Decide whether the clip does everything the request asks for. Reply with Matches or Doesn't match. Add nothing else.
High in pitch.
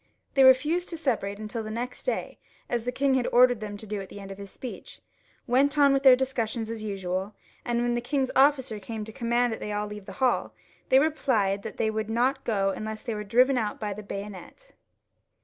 Matches